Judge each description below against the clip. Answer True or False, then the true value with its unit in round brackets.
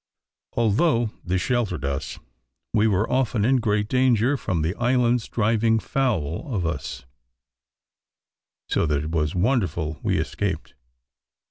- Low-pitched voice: True (105 Hz)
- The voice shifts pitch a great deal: True (6.3 semitones)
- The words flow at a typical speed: False (125 wpm)